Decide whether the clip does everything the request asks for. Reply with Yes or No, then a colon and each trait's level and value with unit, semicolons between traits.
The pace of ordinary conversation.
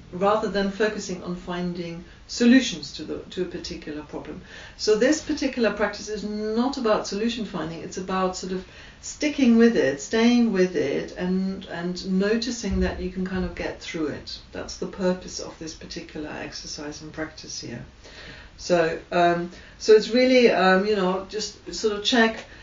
Yes: average, 170 wpm